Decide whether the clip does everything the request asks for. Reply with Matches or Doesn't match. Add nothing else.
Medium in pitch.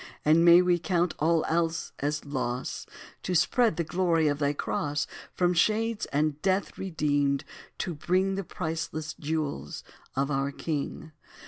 Matches